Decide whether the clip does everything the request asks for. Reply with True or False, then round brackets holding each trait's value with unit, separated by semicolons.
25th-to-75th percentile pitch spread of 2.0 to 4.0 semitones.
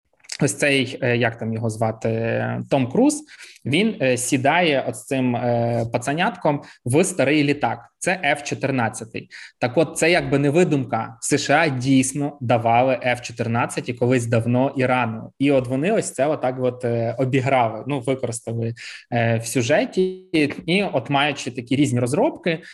True (3.4 semitones)